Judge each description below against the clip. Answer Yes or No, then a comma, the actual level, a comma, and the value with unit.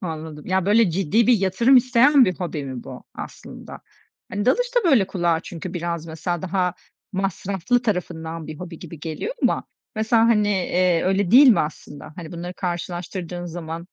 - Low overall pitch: No, medium, 180 Hz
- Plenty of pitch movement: No, average, 4.0 semitones